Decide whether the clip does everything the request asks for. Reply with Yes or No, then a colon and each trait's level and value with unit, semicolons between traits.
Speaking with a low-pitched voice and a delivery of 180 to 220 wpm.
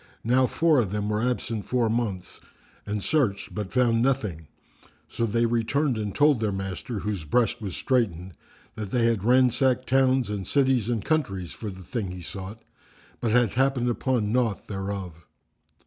No: low, 115 Hz; average, 165 wpm